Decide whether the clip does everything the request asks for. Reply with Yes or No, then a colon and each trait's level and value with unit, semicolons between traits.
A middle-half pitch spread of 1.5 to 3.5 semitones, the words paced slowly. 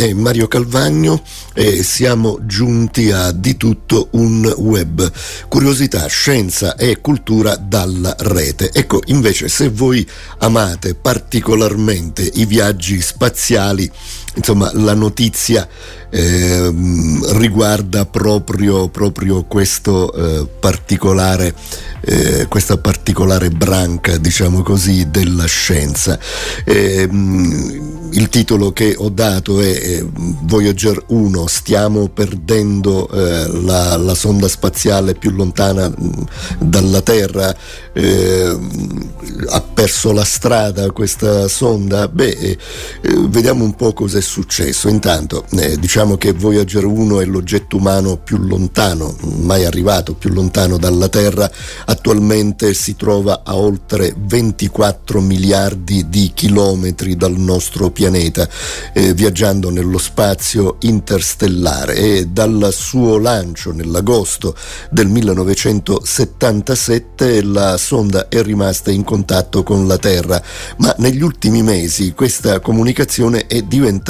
Yes: average, 2.9 semitones; slow, 110 wpm